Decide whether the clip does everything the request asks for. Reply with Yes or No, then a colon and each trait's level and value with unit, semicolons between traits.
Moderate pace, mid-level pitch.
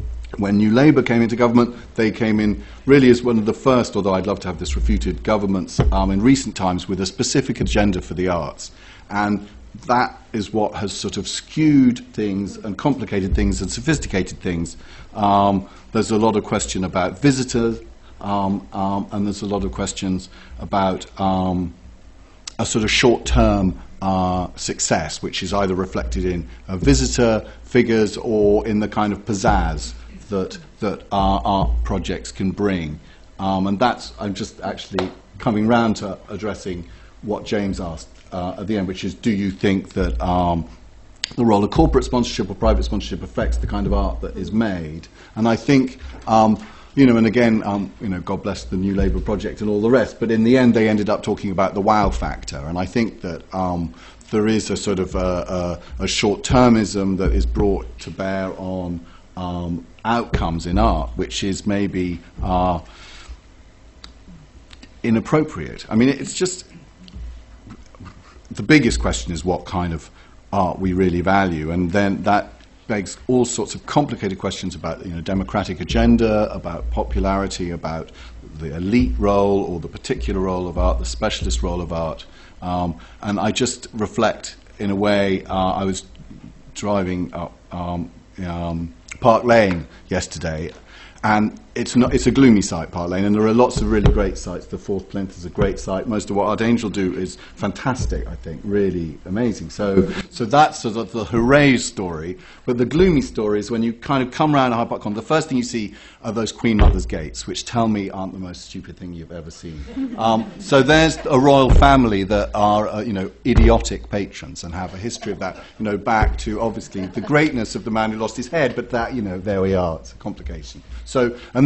No: average, 190 wpm; low, 100 Hz